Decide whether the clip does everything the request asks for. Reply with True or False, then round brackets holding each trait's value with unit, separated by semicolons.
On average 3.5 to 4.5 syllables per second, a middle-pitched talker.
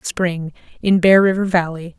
True (4.4 syllables/s; 180 Hz)